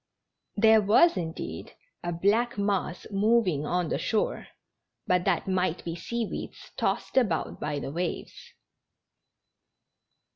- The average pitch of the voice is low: No, high, 190 Hz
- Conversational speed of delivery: No, slow, 120 wpm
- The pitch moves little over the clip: No, average, 4.2 semitones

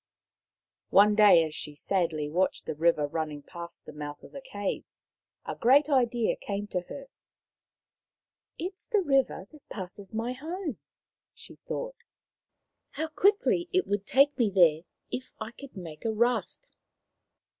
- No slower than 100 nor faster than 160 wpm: Yes, average, 155 wpm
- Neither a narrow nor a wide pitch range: No, wide, 8.5 semitones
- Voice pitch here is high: Yes, high, 215 Hz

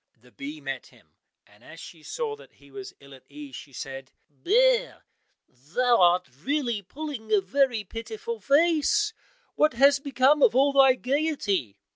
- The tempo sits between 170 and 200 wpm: No, average, 160 wpm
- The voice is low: No, very high, 255 Hz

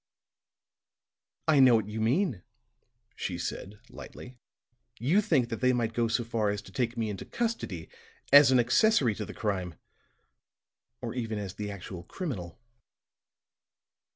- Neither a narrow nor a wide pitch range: Yes, average, 3.9 semitones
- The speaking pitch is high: No, low, 115 Hz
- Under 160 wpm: Yes, average, 145 wpm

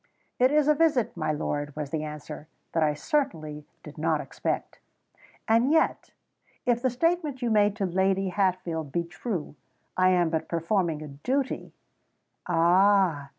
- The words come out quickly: No, average, 145 wpm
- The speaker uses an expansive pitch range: Yes, wide, 7.5 semitones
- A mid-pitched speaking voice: Yes, medium, 180 Hz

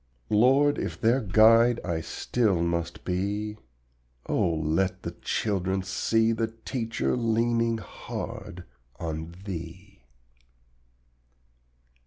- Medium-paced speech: No, slow, 100 wpm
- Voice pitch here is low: Yes, low, 105 Hz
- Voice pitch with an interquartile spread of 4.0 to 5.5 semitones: Yes, average, 4.4 semitones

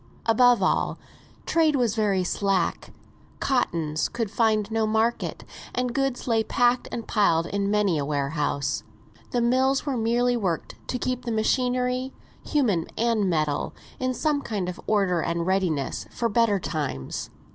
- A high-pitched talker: Yes, high, 220 Hz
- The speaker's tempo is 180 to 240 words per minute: No, average, 145 wpm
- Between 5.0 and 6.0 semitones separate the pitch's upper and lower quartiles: Yes, average, 5.3 semitones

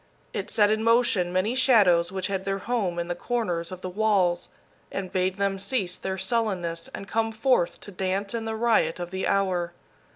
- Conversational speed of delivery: Yes, average, 195 wpm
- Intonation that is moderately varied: Yes, average, 3.7 semitones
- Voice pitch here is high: Yes, high, 195 Hz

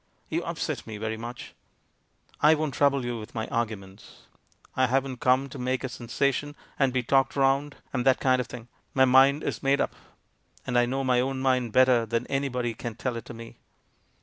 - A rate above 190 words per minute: Yes, fast, 205 wpm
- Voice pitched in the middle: No, low, 130 Hz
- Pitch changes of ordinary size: No, narrow, 2.3 semitones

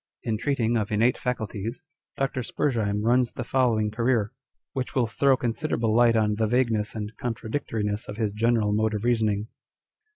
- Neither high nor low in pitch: No, low, 115 Hz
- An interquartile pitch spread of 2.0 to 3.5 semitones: Yes, narrow, 2.4 semitones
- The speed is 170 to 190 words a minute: No, average, 160 wpm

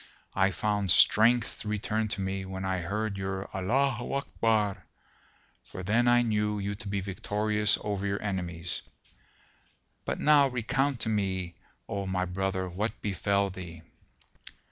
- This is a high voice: No, low, 100 Hz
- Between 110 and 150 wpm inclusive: Yes, average, 140 wpm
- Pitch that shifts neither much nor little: No, narrow, 2.3 semitones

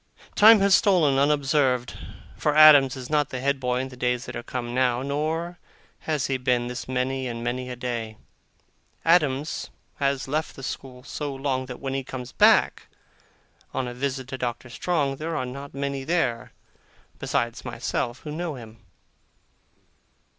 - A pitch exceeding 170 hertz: No, low, 135 Hz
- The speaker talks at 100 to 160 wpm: No, average, 170 wpm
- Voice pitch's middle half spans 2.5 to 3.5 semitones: Yes, average, 2.8 semitones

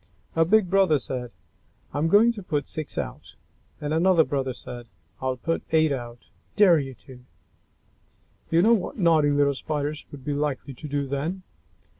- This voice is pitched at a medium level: Yes, medium, 150 Hz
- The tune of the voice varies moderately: Yes, average, 3.7 semitones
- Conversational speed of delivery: Yes, average, 170 wpm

